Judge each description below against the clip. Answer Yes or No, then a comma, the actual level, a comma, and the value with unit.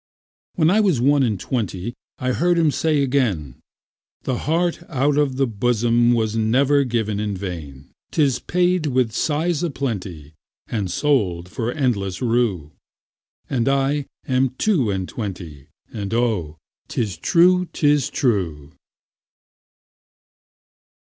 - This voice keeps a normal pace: No, slow, 110 wpm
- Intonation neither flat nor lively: No, wide, 6.4 semitones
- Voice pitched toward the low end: Yes, low, 120 Hz